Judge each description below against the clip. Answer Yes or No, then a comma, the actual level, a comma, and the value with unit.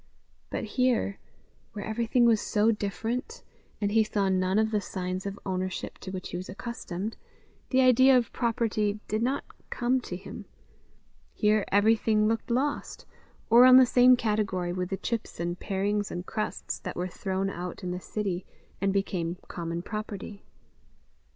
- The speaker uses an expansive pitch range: No, average, 3.5 semitones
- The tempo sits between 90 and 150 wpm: No, average, 160 wpm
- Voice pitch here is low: No, high, 210 Hz